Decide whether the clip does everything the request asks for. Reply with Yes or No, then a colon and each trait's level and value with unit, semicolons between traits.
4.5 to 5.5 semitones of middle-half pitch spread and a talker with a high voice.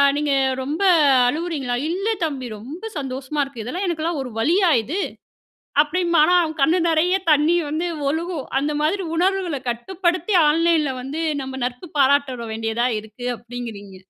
Yes: average, 5.0 semitones; very high, 300 Hz